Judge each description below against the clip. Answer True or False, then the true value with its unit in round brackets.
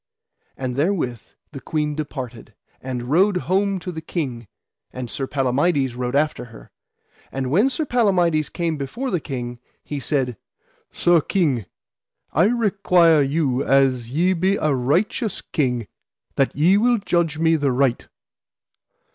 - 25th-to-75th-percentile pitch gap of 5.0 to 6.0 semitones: True (5.5 semitones)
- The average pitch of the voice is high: False (150 Hz)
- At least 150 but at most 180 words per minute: False (140 wpm)